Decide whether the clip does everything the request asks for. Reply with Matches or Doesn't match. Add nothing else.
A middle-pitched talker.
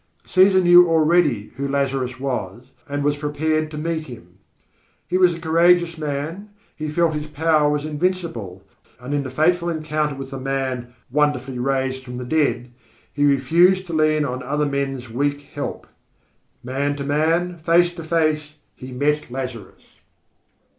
Matches